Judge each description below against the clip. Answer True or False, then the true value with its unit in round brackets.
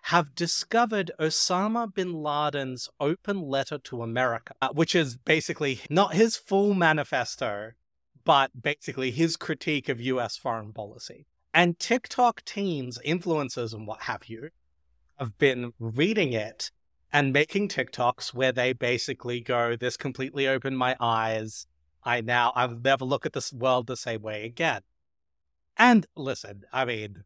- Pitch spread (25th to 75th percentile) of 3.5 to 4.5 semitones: False (5.2 semitones)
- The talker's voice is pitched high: False (135 Hz)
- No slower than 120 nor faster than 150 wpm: True (140 wpm)